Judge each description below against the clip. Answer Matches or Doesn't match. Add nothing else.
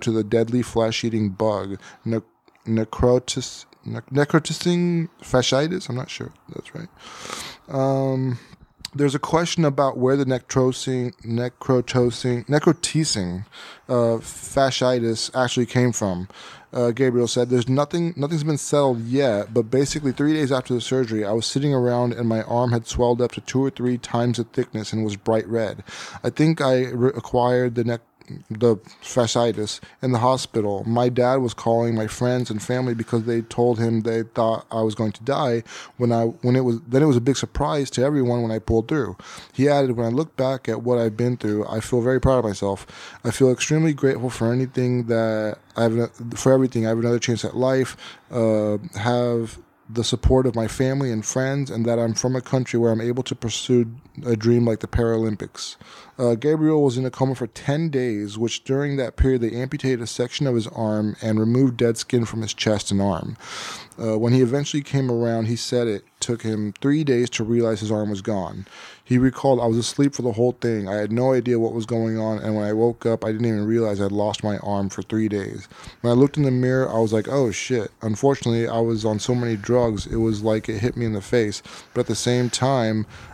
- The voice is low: Matches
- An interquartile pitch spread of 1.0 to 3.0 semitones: Matches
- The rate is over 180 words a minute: Matches